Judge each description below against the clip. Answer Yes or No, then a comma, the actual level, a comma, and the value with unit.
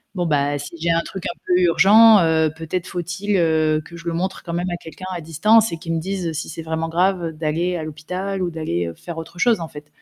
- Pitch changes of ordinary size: No, narrow, 2.3 semitones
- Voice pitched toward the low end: No, medium, 170 Hz